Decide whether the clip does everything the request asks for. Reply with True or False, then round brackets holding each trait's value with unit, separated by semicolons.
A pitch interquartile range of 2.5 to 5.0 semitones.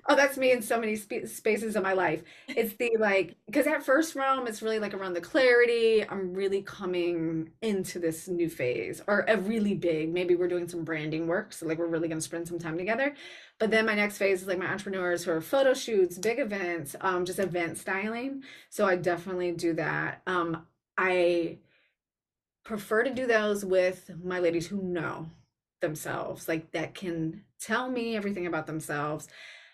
True (4.6 semitones)